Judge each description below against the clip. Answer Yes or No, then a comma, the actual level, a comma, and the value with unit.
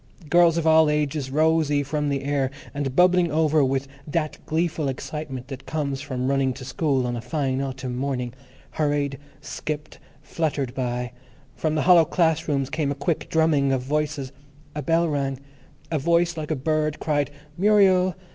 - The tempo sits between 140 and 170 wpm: Yes, average, 165 wpm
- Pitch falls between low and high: Yes, medium, 145 Hz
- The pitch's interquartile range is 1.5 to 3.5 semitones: Yes, average, 2.9 semitones